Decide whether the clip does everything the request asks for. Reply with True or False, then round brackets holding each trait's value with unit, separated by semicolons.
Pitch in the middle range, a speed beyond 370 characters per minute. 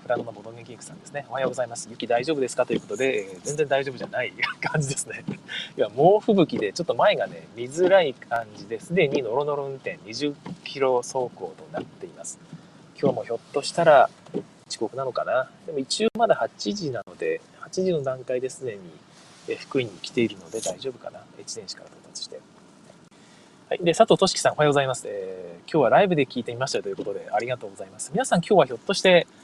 True (145 Hz; 435 characters per minute)